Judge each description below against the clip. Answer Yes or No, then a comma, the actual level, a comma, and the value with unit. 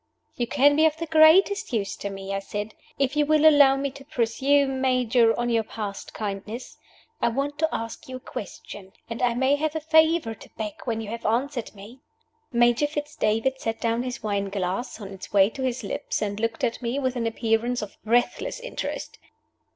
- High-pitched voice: Yes, high, 240 Hz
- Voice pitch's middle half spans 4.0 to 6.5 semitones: Yes, average, 4.4 semitones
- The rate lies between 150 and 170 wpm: No, fast, 205 wpm